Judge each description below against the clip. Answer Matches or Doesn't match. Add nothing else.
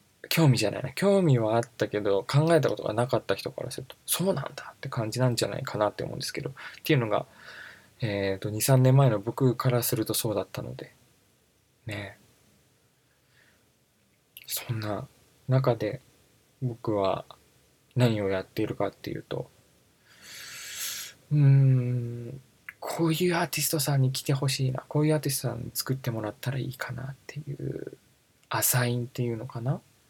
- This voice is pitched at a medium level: Doesn't match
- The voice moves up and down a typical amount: Matches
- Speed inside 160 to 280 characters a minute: Doesn't match